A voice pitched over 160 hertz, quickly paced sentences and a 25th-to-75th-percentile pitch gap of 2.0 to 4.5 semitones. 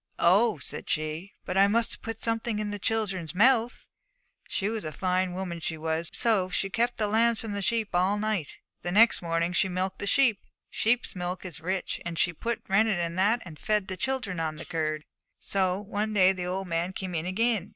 Yes: high, 190 Hz; fast, 210 wpm; average, 3.7 semitones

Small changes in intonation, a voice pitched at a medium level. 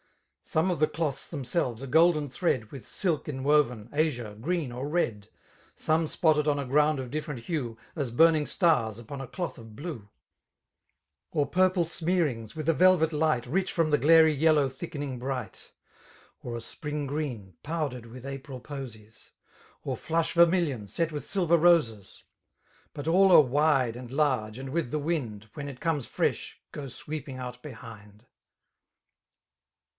No: average, 4.5 semitones; medium, 145 Hz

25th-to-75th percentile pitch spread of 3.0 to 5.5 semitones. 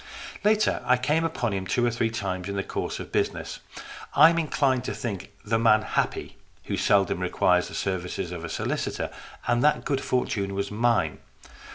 Yes: average, 4.7 semitones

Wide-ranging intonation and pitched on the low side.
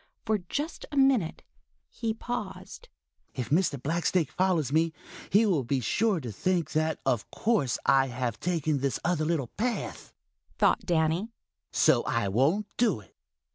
No: wide, 7.2 semitones; medium, 165 Hz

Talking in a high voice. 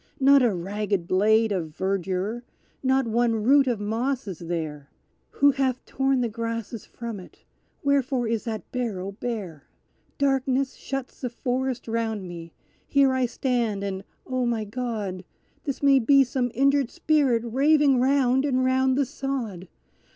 Yes: high, 240 Hz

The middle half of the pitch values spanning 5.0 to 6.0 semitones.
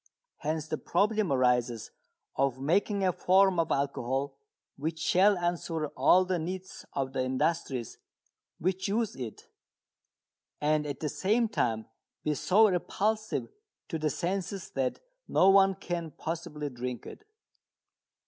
Yes: wide, 5.6 semitones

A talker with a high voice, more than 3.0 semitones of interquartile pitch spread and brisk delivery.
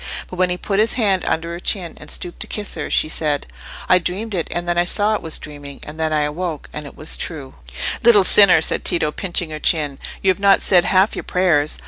No: medium, 175 Hz; average, 3.6 semitones; fast, 235 wpm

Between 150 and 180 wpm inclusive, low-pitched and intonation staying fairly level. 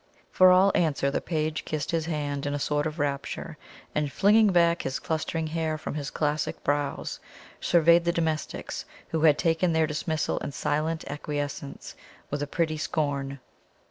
No: average, 165 wpm; medium, 155 Hz; narrow, 2.2 semitones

